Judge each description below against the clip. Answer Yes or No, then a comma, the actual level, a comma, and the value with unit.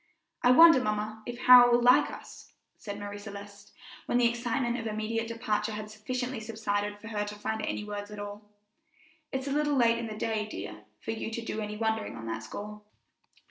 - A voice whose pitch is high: Yes, high, 220 Hz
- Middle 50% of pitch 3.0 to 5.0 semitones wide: No, narrow, 2.4 semitones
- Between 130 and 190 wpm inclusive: No, average, 200 wpm